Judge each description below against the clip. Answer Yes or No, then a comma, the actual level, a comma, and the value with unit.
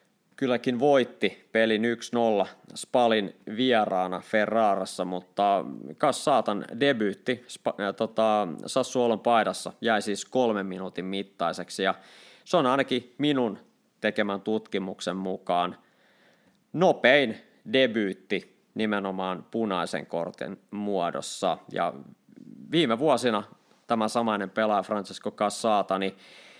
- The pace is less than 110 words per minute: Yes, slow, 95 wpm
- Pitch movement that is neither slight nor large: Yes, average, 3.7 semitones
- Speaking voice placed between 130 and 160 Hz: No, low, 105 Hz